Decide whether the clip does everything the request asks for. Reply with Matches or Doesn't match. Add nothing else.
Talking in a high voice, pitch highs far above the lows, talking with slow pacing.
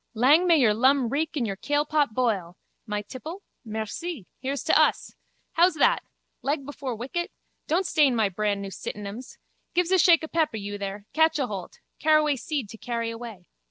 Doesn't match